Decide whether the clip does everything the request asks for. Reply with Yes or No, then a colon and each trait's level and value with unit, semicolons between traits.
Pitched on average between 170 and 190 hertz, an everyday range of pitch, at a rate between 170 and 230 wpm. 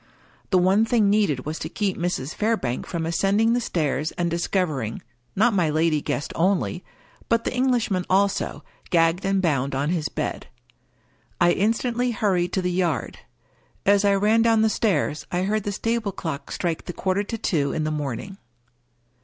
Yes: medium, 185 Hz; average, 4.6 semitones; average, 180 wpm